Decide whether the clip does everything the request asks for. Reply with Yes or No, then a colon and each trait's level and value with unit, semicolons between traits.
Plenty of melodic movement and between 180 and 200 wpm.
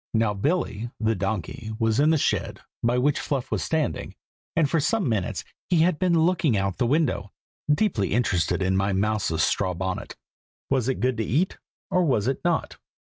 Yes: wide, 7.6 semitones; average, 190 wpm